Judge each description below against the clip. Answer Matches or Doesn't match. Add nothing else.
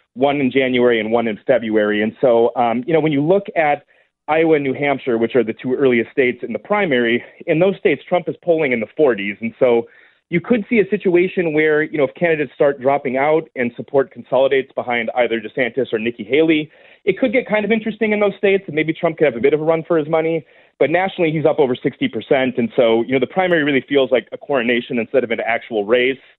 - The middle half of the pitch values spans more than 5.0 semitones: Matches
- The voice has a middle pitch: Matches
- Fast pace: Matches